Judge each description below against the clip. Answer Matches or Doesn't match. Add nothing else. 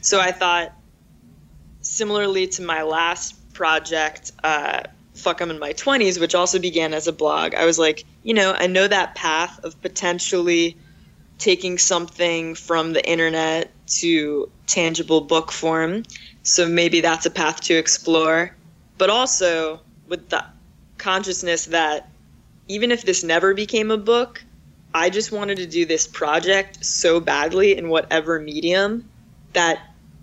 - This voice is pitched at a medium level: Matches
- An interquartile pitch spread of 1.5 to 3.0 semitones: Matches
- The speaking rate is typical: Matches